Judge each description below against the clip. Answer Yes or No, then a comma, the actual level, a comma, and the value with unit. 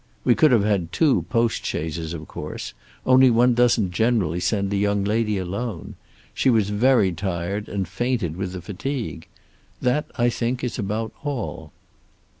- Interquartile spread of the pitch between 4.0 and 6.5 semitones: Yes, average, 4.7 semitones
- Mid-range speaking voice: No, low, 105 Hz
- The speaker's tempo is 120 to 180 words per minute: Yes, average, 155 wpm